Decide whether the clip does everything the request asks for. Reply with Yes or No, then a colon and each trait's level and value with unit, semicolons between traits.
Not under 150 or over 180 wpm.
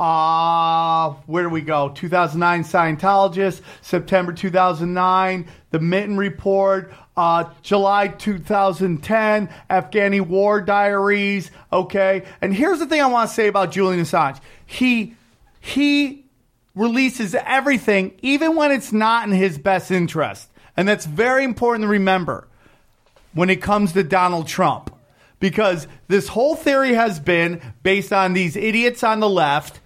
No: slow, 135 wpm